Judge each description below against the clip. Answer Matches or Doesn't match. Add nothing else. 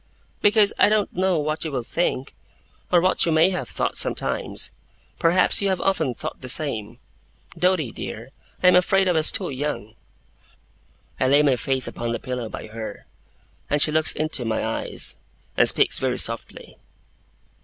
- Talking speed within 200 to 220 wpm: Doesn't match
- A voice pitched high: Doesn't match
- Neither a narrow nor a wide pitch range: Doesn't match